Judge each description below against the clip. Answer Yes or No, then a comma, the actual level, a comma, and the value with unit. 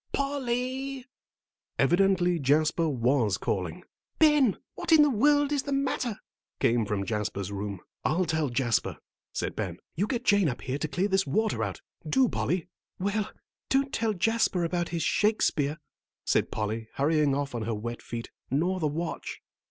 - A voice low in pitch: No, medium, 175 Hz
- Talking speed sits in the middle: Yes, average, 160 wpm